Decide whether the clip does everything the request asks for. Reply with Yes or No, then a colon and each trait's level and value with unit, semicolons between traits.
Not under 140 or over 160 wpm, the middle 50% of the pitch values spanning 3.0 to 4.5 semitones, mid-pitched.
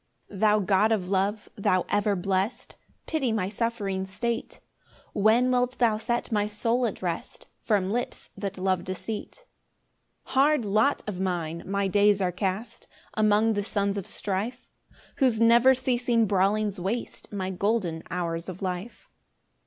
No: average, 150 wpm; average, 3.4 semitones; high, 205 Hz